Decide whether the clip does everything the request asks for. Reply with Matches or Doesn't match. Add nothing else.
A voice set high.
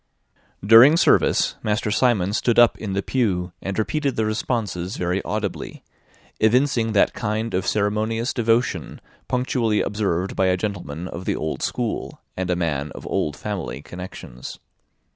Doesn't match